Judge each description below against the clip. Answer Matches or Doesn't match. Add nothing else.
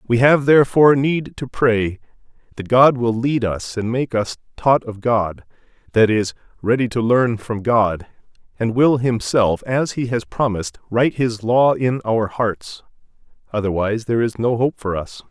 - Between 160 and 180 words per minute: Matches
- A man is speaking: Matches